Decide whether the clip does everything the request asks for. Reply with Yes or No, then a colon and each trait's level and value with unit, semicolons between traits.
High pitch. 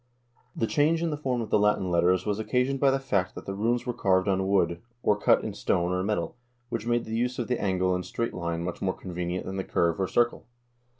No: low, 100 Hz